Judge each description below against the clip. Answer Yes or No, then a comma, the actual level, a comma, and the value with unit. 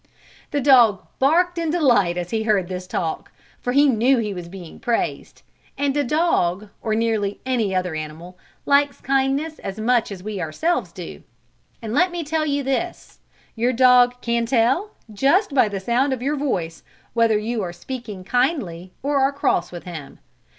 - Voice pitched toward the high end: Yes, high, 235 Hz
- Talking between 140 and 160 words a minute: No, average, 175 wpm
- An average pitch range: No, wide, 6.4 semitones